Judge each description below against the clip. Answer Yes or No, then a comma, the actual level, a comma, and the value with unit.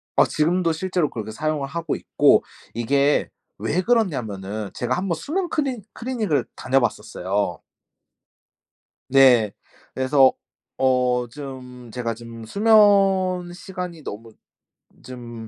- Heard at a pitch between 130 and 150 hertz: Yes, medium, 140 Hz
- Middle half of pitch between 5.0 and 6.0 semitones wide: No, wide, 7.4 semitones